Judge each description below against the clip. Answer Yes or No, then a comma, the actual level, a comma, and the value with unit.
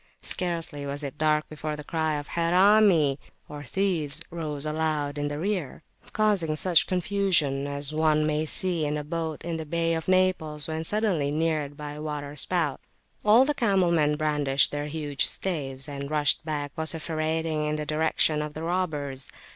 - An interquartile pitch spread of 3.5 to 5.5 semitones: No, narrow, 2.4 semitones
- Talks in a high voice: No, medium, 155 Hz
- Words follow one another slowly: No, average, 170 wpm